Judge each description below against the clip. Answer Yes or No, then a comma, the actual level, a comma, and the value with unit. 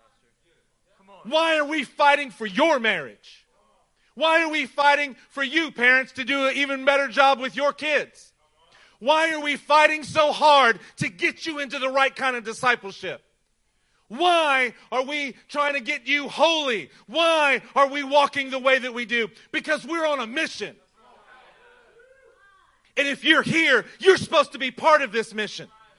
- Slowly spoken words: No, average, 165 wpm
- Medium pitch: No, very high, 280 Hz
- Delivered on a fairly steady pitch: No, average, 3.1 semitones